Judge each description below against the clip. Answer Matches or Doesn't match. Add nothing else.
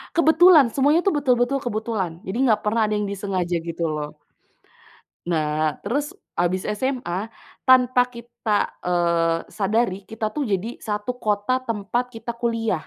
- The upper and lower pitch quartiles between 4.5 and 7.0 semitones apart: Matches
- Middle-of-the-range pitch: Doesn't match